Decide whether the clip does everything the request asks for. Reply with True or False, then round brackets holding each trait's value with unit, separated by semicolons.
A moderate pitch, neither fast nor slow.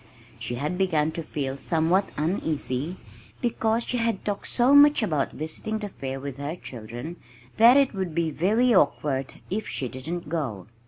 True (165 Hz; 165 wpm)